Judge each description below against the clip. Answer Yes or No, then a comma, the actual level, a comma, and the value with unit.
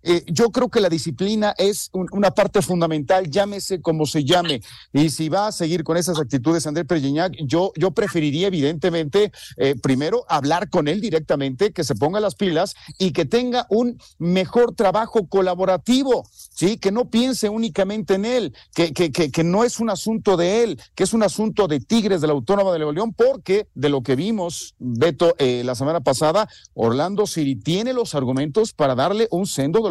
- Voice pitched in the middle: Yes, medium, 180 Hz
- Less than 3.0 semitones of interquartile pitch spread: No, average, 5.2 semitones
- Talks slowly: No, fast, 190 wpm